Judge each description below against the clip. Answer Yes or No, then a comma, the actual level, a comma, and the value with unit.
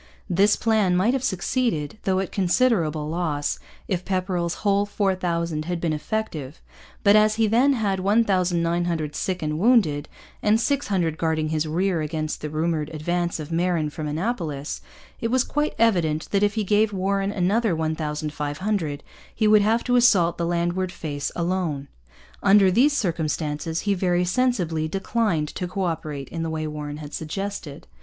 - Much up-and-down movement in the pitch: No, average, 4.6 semitones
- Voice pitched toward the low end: No, medium, 175 Hz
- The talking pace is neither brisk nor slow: Yes, average, 160 wpm